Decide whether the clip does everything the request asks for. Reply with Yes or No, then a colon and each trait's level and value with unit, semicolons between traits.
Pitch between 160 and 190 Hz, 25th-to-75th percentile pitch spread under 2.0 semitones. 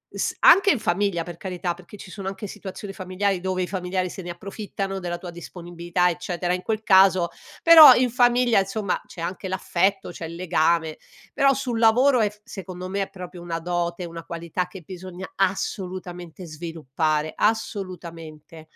No: medium, 185 Hz; narrow, 2.4 semitones